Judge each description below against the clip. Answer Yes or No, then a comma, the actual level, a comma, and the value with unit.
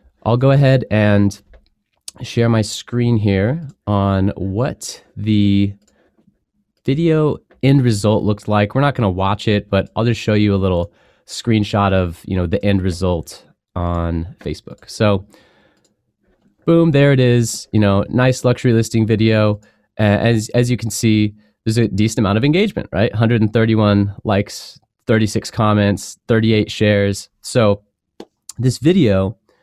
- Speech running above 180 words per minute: No, average, 140 wpm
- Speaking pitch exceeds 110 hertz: No, low, 105 Hz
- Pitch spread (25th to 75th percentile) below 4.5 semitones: Yes, average, 2.8 semitones